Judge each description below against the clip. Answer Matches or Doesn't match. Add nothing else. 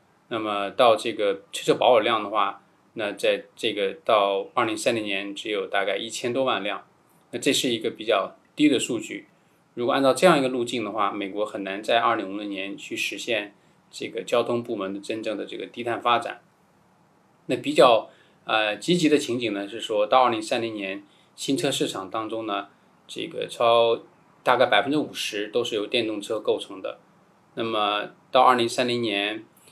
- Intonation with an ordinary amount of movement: Doesn't match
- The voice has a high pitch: Doesn't match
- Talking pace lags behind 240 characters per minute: Doesn't match